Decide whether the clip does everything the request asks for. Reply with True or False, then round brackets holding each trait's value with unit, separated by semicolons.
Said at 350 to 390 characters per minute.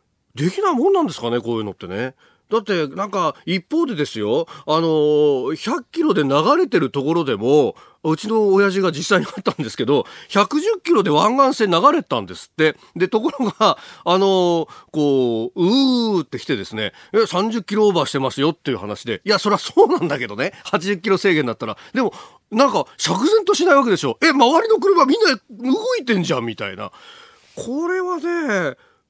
True (360 characters per minute)